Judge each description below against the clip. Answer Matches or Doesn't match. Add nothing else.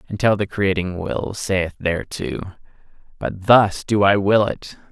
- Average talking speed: Matches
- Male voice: Matches